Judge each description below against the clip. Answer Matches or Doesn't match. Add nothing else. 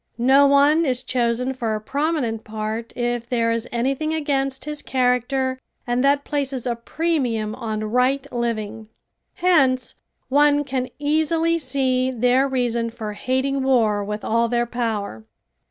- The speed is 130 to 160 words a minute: Matches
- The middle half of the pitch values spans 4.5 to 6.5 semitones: Doesn't match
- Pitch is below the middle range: Doesn't match